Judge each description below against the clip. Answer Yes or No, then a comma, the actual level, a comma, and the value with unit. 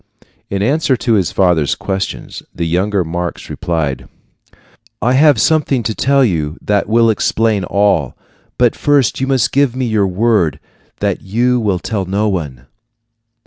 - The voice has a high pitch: No, low, 105 Hz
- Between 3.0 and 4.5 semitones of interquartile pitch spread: No, average, 5.3 semitones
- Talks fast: No, average, 150 wpm